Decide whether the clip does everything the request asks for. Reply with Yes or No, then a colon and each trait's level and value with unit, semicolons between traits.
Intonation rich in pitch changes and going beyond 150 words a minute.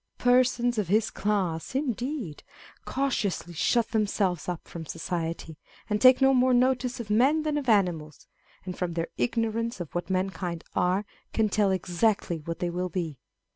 Yes: wide, 5.7 semitones; average, 165 wpm